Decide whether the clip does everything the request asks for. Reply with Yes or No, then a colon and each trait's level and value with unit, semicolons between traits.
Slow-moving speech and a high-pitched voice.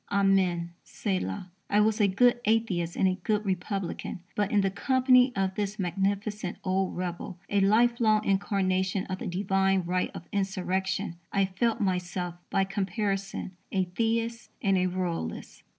No: average, 150 wpm; high, 195 Hz